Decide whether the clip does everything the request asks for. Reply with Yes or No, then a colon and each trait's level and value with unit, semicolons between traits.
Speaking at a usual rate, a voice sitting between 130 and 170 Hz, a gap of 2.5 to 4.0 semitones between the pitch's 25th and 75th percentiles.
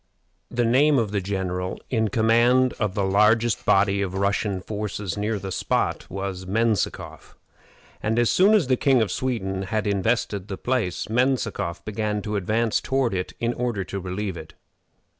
No: average, 165 wpm; low, 105 Hz; average, 3.4 semitones